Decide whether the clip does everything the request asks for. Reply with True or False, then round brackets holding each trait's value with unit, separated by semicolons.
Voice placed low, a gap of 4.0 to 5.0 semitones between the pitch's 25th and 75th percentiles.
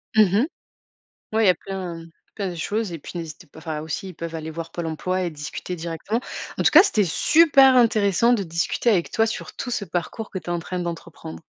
False (180 Hz; 4.7 semitones)